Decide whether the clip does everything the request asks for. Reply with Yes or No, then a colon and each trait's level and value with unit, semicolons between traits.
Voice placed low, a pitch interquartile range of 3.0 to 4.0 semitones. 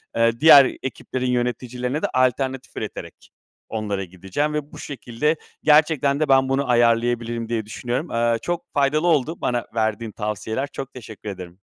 Yes: low, 125 Hz; average, 3.4 semitones